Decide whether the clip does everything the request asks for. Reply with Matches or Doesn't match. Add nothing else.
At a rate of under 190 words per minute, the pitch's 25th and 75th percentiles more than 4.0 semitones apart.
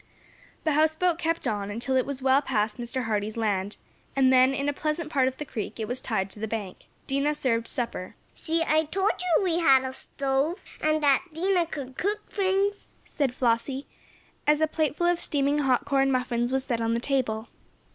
Doesn't match